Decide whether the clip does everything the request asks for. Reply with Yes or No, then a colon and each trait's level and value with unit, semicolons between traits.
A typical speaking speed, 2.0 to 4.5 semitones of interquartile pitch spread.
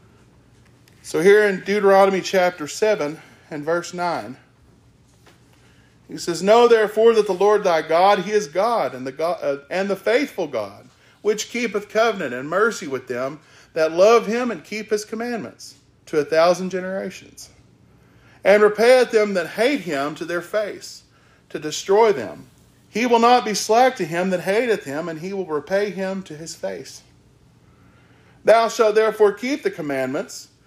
No: average, 160 wpm; average, 5.3 semitones